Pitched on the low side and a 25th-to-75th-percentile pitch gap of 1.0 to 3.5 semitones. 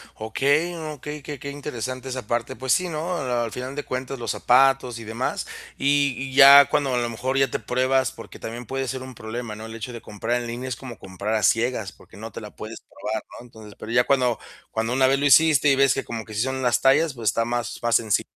Yes: low, 125 Hz; average, 2.9 semitones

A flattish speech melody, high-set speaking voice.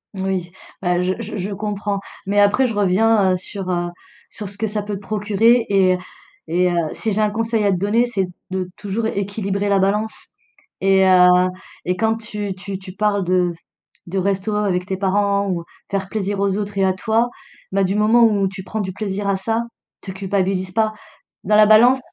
Yes: narrow, 2.1 semitones; high, 200 Hz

